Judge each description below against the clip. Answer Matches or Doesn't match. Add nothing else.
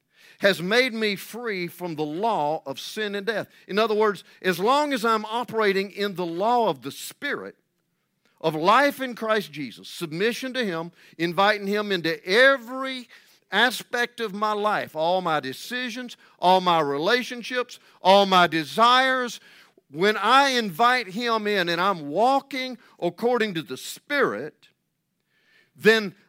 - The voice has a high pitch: Matches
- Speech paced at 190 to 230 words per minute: Doesn't match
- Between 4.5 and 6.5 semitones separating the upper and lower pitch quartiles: Matches